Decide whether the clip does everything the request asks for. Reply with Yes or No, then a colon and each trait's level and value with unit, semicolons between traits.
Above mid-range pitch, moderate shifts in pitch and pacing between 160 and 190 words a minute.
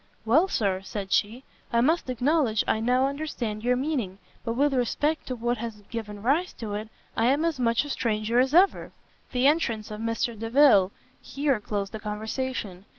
Yes: high, 235 Hz; average, 4.2 semitones; average, 180 wpm